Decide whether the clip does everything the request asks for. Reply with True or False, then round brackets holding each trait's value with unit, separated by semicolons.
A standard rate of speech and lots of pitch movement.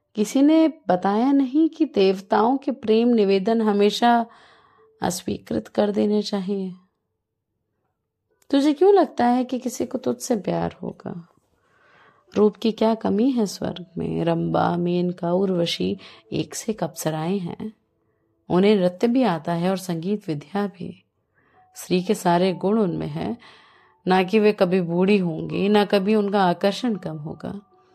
False (140 wpm; 4.8 semitones)